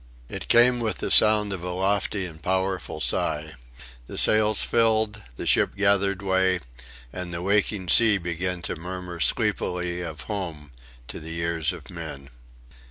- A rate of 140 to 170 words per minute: Yes, average, 155 wpm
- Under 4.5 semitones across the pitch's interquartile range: Yes, average, 3.3 semitones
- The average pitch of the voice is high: No, very low, 95 Hz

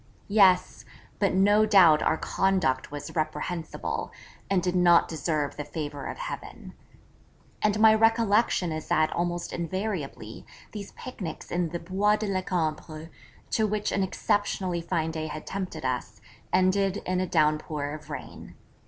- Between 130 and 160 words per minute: Yes, average, 145 wpm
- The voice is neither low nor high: Yes, medium, 180 Hz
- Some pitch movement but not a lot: Yes, average, 4.1 semitones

